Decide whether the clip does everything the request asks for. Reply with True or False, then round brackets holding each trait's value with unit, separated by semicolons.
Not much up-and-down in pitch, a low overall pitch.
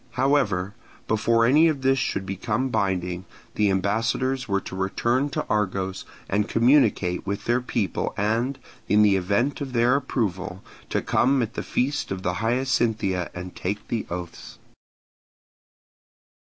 False (4.9 semitones; 110 Hz)